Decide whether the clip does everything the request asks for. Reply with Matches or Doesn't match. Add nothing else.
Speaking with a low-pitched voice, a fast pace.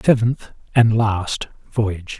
Doesn't match